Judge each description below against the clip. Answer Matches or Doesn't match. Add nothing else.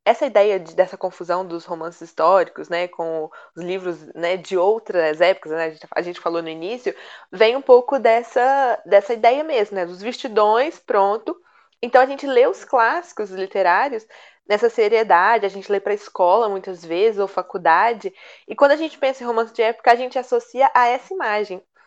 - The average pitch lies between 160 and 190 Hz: Doesn't match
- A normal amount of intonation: Doesn't match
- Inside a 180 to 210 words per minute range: Matches